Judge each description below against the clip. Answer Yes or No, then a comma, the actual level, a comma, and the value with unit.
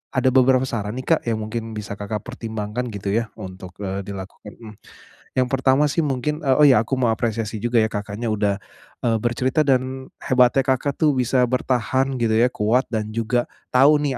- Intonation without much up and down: No, average, 3.4 semitones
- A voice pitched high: No, low, 120 Hz